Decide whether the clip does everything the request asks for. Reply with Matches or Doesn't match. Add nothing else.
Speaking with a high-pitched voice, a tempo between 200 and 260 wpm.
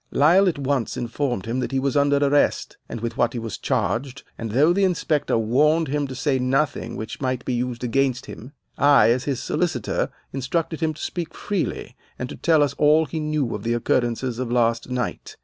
Doesn't match